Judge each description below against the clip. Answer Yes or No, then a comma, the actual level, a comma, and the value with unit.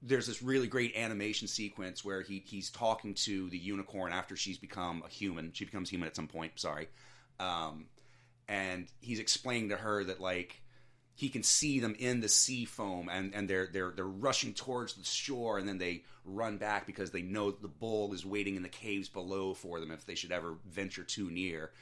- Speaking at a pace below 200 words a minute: No, fast, 205 wpm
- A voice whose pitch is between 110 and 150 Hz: No, low, 100 Hz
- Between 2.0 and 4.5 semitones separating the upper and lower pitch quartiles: Yes, average, 3.4 semitones